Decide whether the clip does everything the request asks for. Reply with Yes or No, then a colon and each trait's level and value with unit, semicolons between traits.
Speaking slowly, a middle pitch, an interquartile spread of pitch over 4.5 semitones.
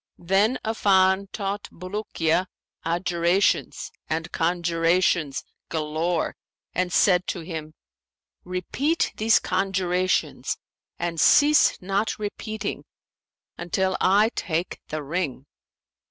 No: slow, 90 wpm; medium, 180 Hz; average, 2.9 semitones